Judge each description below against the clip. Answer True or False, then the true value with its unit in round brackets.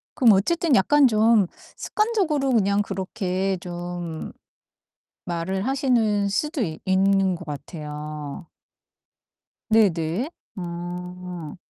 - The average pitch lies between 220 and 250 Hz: False (190 Hz)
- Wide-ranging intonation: False (4.6 semitones)